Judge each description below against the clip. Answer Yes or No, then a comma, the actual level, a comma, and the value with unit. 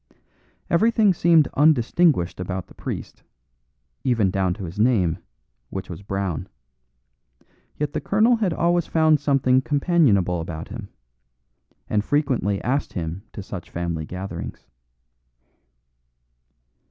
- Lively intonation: Yes, wide, 9.0 semitones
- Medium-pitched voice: No, low, 110 Hz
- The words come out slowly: Yes, slow, 115 wpm